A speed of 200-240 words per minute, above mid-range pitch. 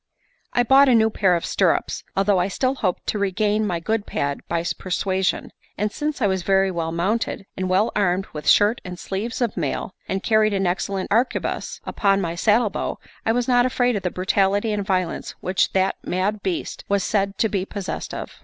Yes: fast, 205 wpm; high, 195 Hz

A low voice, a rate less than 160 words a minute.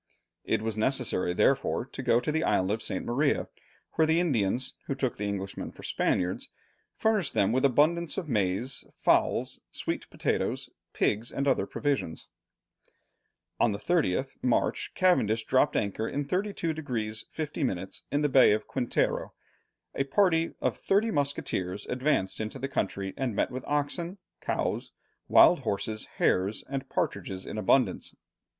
Yes: low, 130 Hz; average, 150 wpm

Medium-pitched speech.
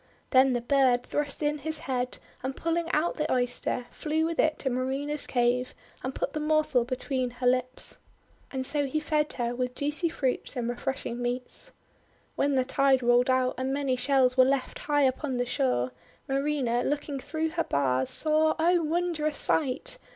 No: very high, 270 Hz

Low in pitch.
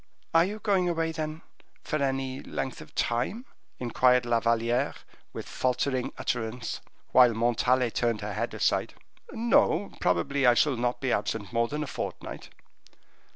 Yes: low, 125 Hz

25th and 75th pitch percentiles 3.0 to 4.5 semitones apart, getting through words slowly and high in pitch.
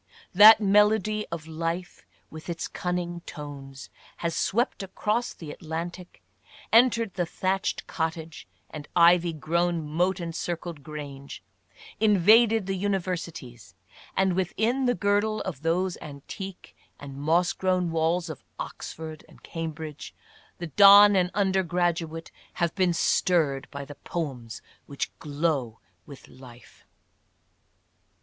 No: average, 3.6 semitones; slow, 130 wpm; medium, 170 Hz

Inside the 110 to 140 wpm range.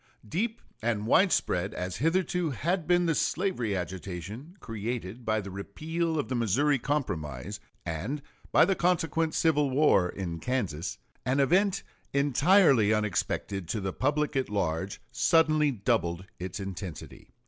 Yes: slow, 135 wpm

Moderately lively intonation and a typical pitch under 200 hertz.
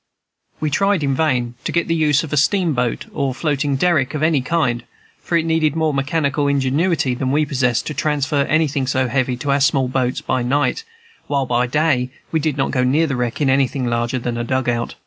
Yes: average, 3.4 semitones; medium, 140 Hz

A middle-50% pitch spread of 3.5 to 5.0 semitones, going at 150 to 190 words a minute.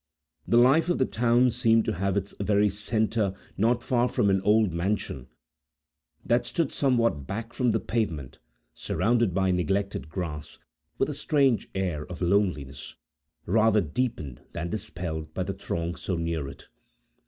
No: wide, 5.4 semitones; average, 155 wpm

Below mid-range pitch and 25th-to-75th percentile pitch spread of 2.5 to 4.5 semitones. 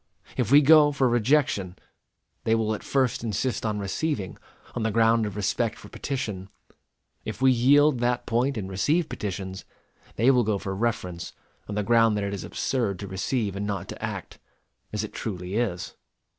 Yes: low, 115 Hz; average, 4.2 semitones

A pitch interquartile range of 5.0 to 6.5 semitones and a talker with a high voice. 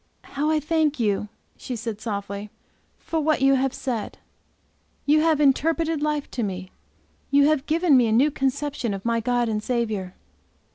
Yes: wide, 5.5 semitones; very high, 265 Hz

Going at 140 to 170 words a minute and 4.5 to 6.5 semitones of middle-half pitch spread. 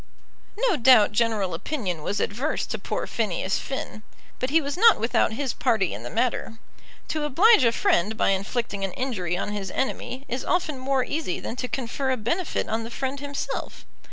No: average, 185 wpm; average, 5.2 semitones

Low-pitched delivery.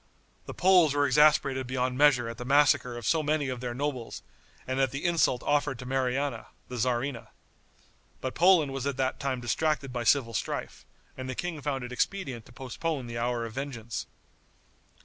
Yes: low, 130 Hz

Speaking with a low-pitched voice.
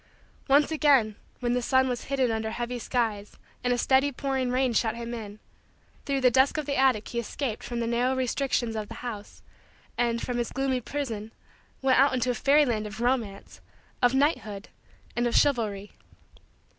No: high, 245 Hz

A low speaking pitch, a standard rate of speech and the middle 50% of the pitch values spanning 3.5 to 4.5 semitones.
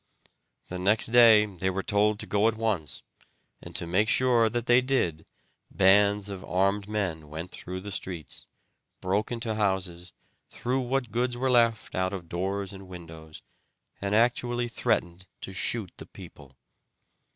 Yes: low, 100 Hz; average, 155 wpm; average, 3.9 semitones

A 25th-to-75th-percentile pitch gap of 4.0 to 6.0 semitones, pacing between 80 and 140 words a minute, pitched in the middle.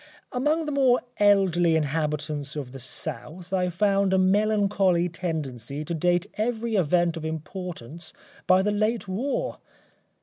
Yes: average, 4.5 semitones; slow, 135 wpm; medium, 180 Hz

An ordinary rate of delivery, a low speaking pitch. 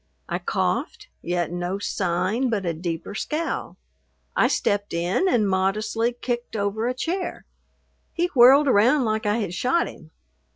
No: average, 150 wpm; high, 215 Hz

